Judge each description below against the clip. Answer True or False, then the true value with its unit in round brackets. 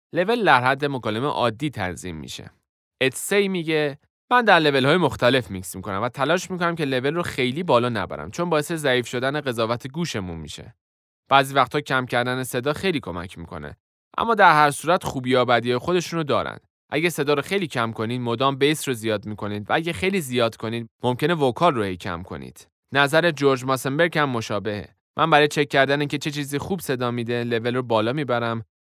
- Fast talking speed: True (185 wpm)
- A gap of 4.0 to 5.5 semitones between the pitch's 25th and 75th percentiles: True (5.1 semitones)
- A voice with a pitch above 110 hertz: True (130 Hz)